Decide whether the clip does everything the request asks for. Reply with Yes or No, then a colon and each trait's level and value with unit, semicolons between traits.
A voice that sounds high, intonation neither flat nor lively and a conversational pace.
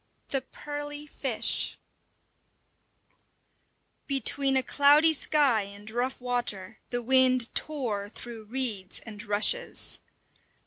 No: very high, 255 Hz; average, 4.5 semitones; slow, 100 wpm